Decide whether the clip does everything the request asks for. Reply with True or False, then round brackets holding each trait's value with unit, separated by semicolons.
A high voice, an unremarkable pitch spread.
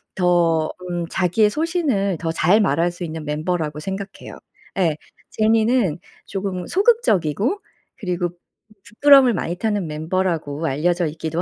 False (180 Hz; 4.5 semitones)